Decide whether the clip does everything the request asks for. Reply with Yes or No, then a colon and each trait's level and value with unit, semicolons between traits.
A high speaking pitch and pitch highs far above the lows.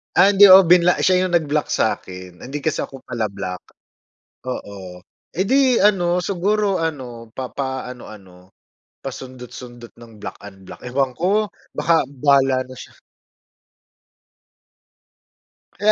No: low, 135 Hz; wide, 7.4 semitones